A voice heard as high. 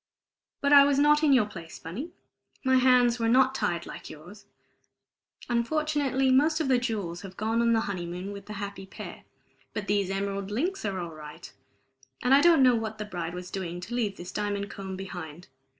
Yes: high, 210 Hz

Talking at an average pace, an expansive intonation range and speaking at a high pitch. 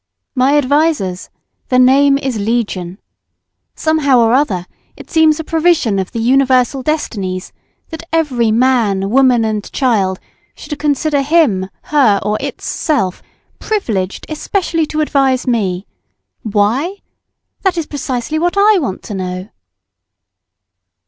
No: slow, 120 wpm; wide, 6.5 semitones; very high, 255 Hz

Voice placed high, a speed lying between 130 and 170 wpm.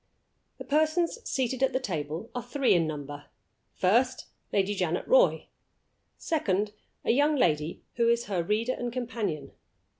Yes: high, 230 Hz; average, 145 wpm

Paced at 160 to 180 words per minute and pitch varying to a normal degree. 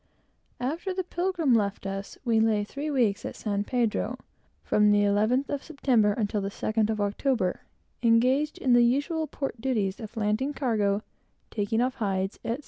Yes: average, 165 wpm; average, 4.4 semitones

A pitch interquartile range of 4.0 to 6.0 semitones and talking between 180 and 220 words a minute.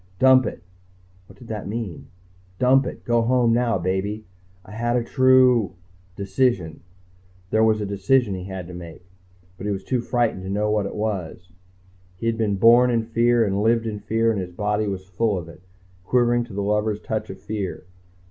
No: average, 3.4 semitones; average, 195 wpm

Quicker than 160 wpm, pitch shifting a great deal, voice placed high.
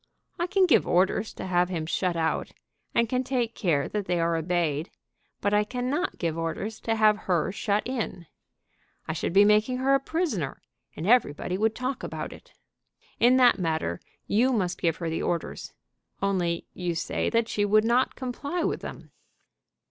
Yes: average, 180 wpm; wide, 6.3 semitones; high, 205 Hz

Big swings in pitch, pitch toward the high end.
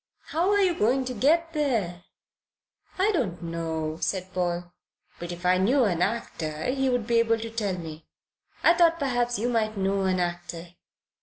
Yes: wide, 6.7 semitones; high, 210 Hz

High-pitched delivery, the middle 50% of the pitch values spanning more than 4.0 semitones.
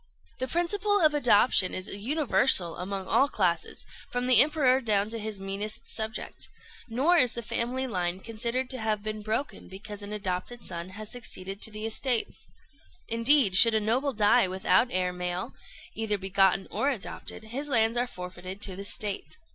Yes: high, 220 Hz; average, 4.4 semitones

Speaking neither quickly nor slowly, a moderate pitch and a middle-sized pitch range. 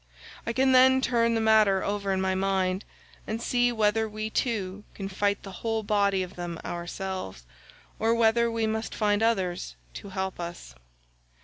No: average, 170 wpm; high, 205 Hz; average, 3.0 semitones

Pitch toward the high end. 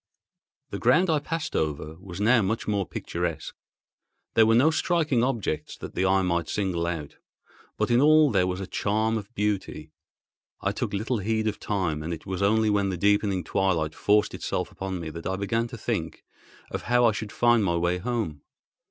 No: low, 100 Hz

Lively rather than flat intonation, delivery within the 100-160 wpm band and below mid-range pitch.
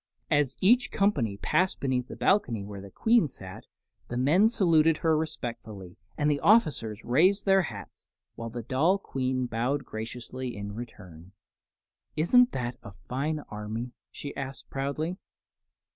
Yes: wide, 6.0 semitones; average, 145 wpm; low, 130 Hz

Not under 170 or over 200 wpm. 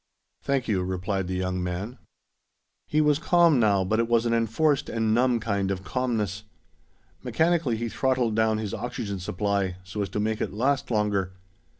Yes: average, 175 wpm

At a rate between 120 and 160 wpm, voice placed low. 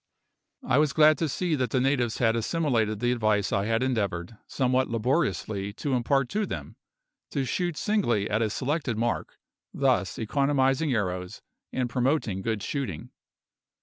Yes: average, 150 wpm; low, 125 Hz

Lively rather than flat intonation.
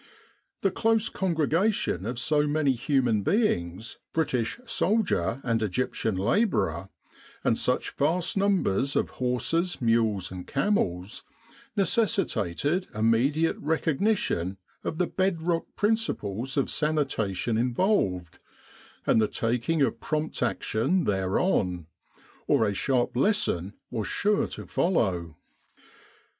Yes: wide, 9.0 semitones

